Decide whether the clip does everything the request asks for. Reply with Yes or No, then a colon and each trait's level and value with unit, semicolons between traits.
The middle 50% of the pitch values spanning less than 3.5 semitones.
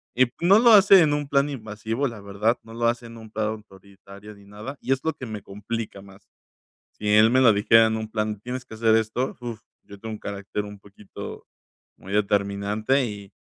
Yes: average, 3.0 semitones